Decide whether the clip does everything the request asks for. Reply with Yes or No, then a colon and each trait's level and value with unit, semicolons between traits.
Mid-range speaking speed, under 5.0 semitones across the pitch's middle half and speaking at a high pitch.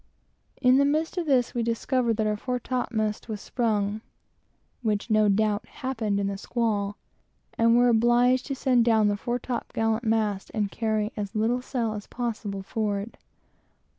Yes: average, 165 wpm; average, 2.7 semitones; high, 225 Hz